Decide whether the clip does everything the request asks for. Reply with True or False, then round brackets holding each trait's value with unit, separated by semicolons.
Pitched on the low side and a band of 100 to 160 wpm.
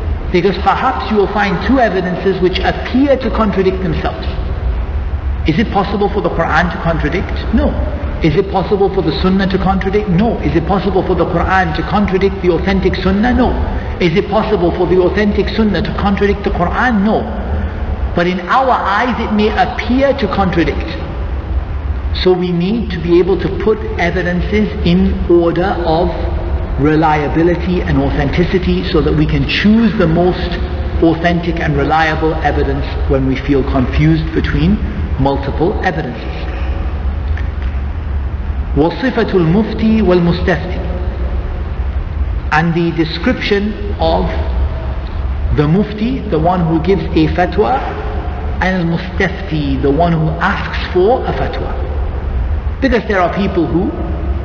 False (160 Hz; 140 wpm)